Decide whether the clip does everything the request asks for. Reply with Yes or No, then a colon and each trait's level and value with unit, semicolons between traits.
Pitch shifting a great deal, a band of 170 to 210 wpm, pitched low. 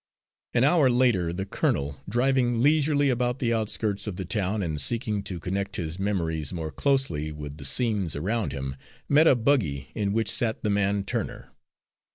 Yes: wide, 6.6 semitones; average, 175 wpm; low, 100 Hz